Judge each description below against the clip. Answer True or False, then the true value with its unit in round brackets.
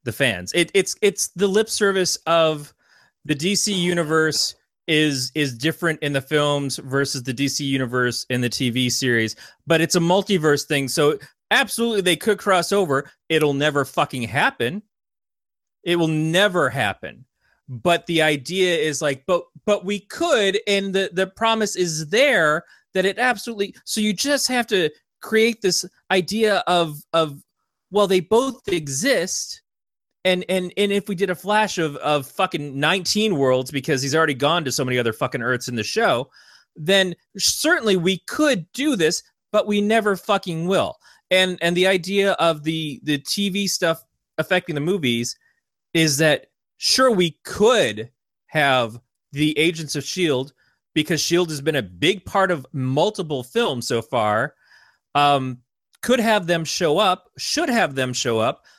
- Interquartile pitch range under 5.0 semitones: False (5.6 semitones)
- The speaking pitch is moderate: True (170 Hz)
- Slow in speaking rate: False (160 wpm)